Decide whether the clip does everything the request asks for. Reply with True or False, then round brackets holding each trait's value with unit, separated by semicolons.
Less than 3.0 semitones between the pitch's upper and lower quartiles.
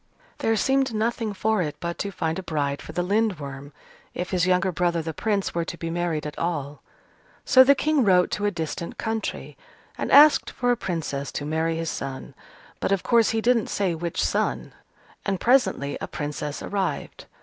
False (5.4 semitones)